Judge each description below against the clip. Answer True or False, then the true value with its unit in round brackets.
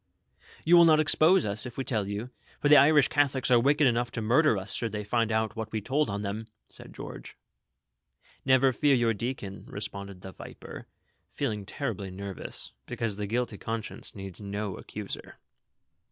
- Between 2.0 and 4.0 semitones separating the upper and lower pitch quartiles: False (4.6 semitones)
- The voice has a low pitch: True (115 Hz)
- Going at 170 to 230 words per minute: True (180 wpm)